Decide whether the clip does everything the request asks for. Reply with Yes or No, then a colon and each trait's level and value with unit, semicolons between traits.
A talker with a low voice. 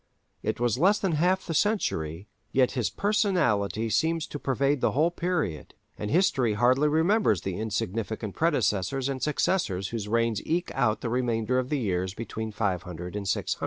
Yes: low, 120 Hz